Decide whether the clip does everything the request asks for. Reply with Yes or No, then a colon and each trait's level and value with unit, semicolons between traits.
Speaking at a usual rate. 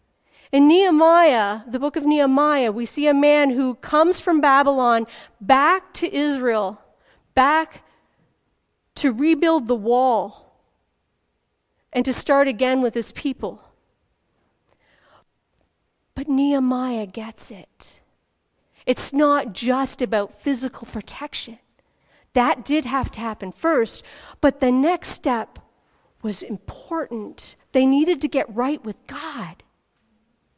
No: slow, 115 wpm